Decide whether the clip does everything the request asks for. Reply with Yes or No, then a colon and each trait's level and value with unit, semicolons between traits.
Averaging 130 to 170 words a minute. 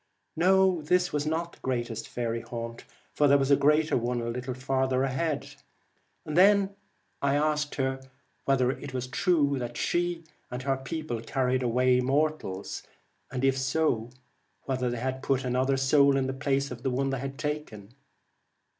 Yes: average, 165 wpm